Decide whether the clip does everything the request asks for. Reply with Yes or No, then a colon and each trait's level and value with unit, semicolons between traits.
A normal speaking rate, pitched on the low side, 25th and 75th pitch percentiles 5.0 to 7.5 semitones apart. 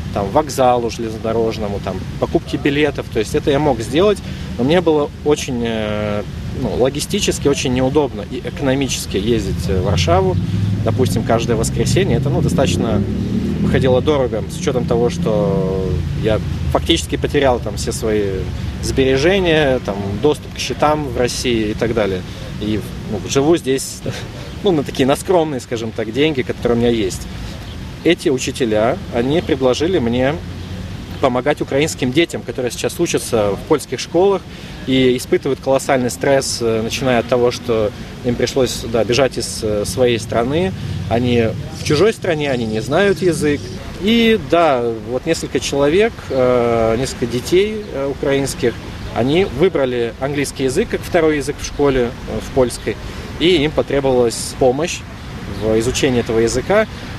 No: average, 140 wpm; low, 125 Hz; average, 4.6 semitones